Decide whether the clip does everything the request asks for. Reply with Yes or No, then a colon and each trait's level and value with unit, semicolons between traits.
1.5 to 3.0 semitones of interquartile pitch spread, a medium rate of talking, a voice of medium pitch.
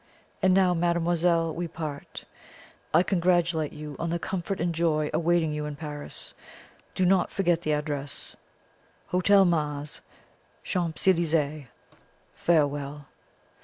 No: narrow, 2.6 semitones; slow, 120 wpm; medium, 165 Hz